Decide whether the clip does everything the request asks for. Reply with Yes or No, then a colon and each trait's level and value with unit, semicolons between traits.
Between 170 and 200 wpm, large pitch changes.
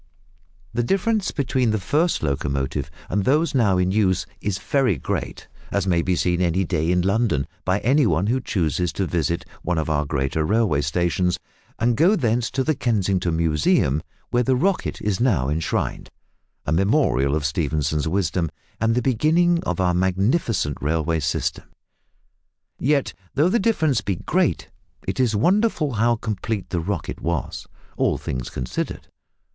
No: average, 160 wpm; wide, 7.3 semitones